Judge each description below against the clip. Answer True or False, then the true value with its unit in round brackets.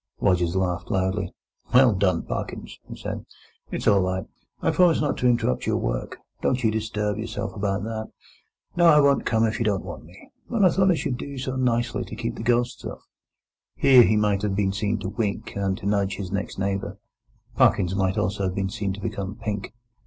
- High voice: False (105 Hz)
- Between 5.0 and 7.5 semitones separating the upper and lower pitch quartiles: False (3.7 semitones)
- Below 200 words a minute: False (205 wpm)